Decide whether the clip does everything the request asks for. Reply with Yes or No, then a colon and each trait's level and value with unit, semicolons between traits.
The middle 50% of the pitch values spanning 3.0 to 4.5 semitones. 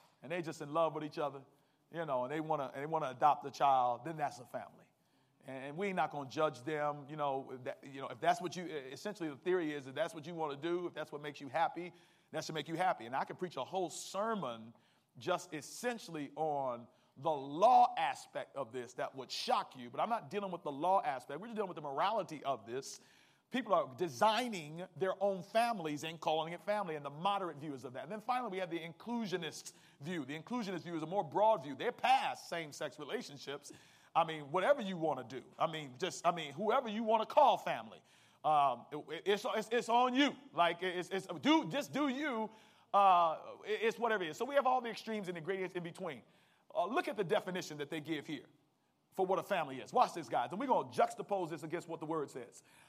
No: wide, 5.4 semitones